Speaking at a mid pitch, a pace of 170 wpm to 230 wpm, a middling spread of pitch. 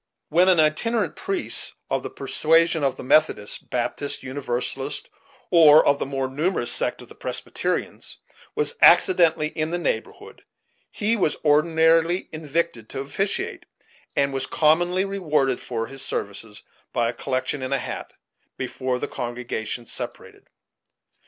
No: medium, 150 Hz; average, 140 wpm; average, 4.5 semitones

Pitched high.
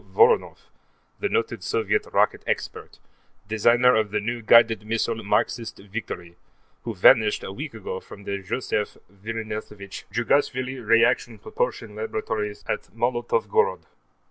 No: low, 115 Hz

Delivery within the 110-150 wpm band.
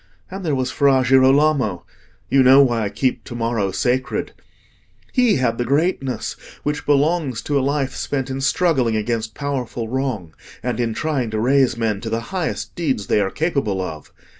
No: average, 170 wpm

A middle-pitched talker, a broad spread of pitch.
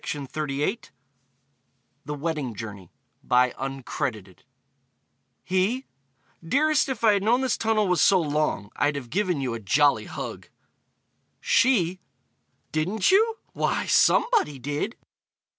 Yes: medium, 170 Hz; wide, 7.7 semitones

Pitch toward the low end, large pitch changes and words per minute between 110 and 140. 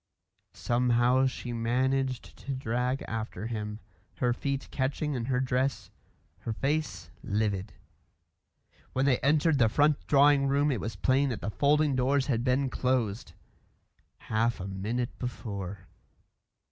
No: low, 125 Hz; average, 3.3 semitones; slow, 135 wpm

